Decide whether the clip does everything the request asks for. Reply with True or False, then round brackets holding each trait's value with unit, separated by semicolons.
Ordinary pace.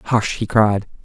True (175 wpm)